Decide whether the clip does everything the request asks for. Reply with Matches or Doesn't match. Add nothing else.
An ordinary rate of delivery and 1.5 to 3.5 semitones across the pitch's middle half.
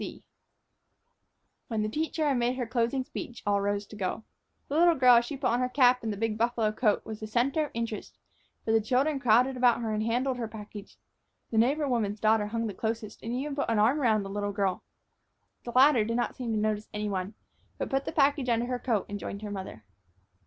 Doesn't match